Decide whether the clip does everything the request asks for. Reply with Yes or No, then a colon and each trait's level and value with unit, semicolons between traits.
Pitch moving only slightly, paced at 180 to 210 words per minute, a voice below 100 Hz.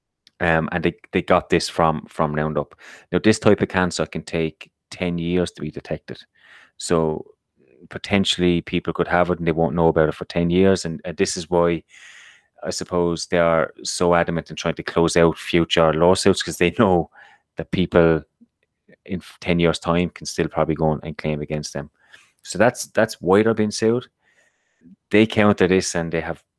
Yes: narrow, 1.9 semitones; average, 190 wpm; very low, 85 Hz